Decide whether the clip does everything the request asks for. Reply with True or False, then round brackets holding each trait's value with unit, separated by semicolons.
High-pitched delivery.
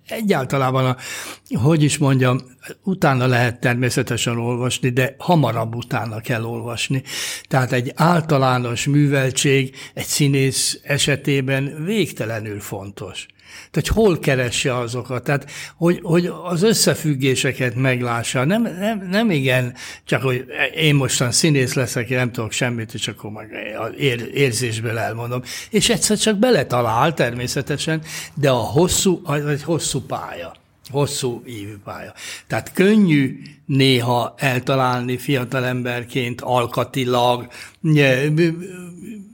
False (135 Hz)